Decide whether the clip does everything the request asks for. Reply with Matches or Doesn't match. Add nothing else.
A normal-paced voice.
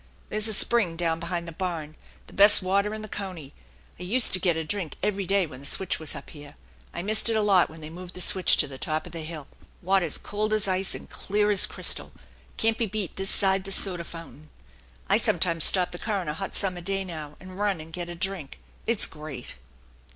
Doesn't match